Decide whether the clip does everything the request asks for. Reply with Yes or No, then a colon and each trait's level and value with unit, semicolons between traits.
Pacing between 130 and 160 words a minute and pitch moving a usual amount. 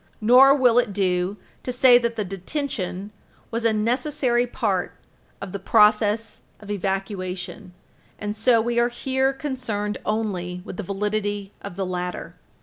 Yes: average, 145 wpm; average, 3.7 semitones